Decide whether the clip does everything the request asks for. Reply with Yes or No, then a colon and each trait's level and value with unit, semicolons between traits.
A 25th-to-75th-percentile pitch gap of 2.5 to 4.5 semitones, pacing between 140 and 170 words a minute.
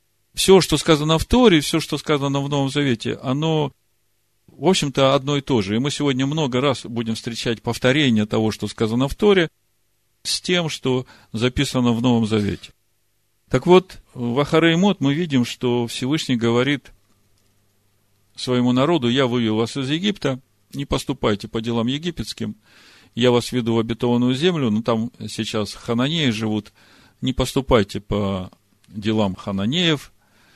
Yes: average, 4.2 semitones; average, 145 wpm